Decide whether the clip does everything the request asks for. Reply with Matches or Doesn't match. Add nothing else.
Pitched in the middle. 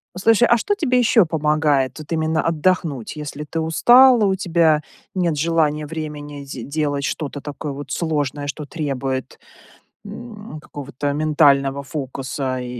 Matches